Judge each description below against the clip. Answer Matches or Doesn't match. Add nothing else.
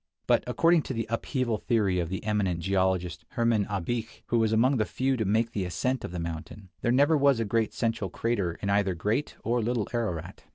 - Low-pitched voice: Matches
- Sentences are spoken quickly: Matches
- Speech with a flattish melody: Doesn't match